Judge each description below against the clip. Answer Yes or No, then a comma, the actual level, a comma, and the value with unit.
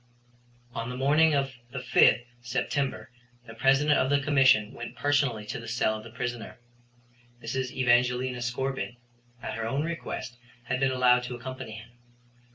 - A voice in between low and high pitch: No, low, 125 Hz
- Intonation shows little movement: Yes, narrow, 2.2 semitones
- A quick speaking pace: No, average, 160 wpm